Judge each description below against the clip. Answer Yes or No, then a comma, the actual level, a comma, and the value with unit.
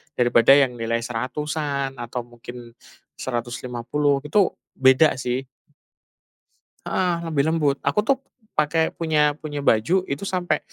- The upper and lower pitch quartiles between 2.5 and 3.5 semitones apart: No, average, 4.1 semitones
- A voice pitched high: No, medium, 140 Hz